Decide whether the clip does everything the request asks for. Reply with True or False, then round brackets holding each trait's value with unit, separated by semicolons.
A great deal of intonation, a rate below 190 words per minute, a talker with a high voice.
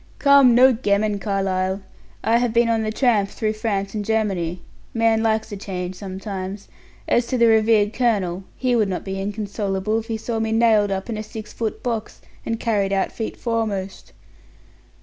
False (2.6 semitones; 180 wpm; 215 Hz)